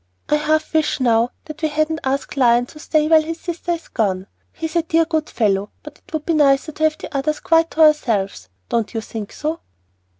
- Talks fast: Yes, fast, 220 wpm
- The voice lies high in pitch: Yes, very high, 305 Hz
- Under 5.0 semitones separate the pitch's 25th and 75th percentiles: Yes, average, 4.6 semitones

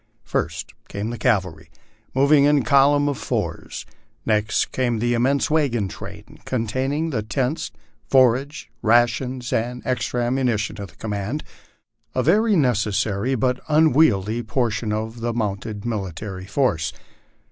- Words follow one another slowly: Yes, slow, 130 wpm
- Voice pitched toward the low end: Yes, low, 120 Hz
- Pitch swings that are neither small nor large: Yes, average, 4.0 semitones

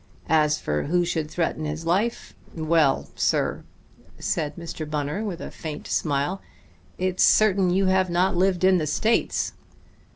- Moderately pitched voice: Yes, medium, 170 Hz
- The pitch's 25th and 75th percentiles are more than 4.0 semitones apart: No, average, 3.5 semitones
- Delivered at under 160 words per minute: Yes, average, 150 wpm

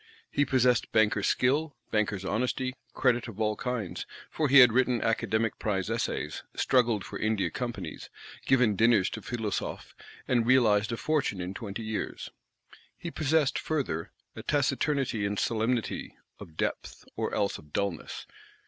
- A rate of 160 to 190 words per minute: No, average, 145 wpm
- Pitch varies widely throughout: No, average, 3.6 semitones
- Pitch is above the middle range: No, low, 115 Hz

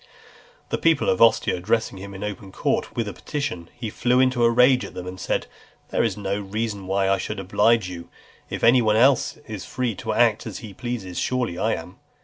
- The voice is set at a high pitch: No, low, 105 Hz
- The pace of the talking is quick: Yes, fast, 215 wpm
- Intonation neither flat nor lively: Yes, average, 3.9 semitones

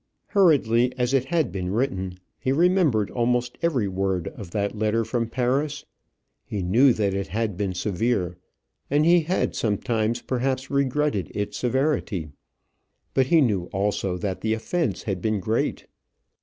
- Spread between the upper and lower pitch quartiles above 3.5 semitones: Yes, average, 5.2 semitones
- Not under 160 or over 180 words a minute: No, average, 150 wpm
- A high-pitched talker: No, low, 115 Hz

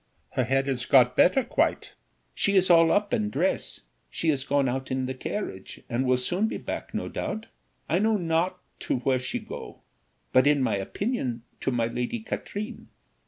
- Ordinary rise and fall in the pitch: No, wide, 6.8 semitones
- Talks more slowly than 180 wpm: No, average, 185 wpm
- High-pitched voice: No, low, 135 Hz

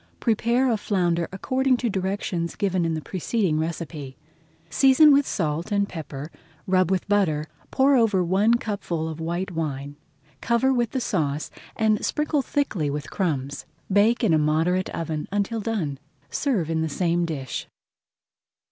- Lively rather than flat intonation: Yes, wide, 6.0 semitones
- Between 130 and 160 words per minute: Yes, average, 150 wpm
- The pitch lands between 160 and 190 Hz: Yes, medium, 185 Hz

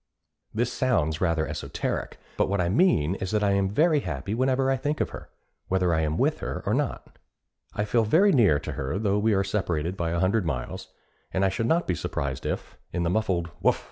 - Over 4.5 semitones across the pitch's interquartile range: Yes, average, 5.2 semitones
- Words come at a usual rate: No, fast, 215 wpm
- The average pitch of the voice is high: No, very low, 95 Hz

